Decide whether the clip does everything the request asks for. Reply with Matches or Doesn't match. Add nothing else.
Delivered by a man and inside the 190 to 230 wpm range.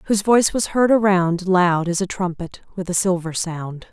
Doesn't match